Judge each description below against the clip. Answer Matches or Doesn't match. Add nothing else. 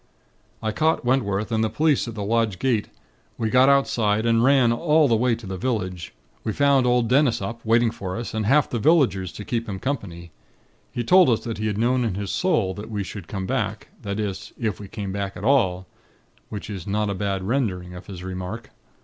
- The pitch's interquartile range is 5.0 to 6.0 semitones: Doesn't match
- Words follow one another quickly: Matches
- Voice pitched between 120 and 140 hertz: Doesn't match